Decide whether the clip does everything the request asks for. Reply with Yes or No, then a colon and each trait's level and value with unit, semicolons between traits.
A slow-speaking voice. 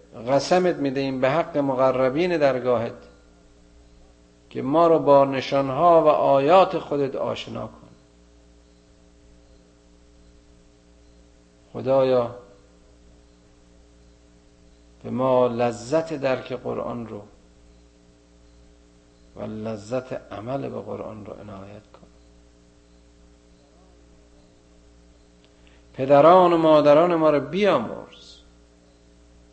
Yes: slow, 75 wpm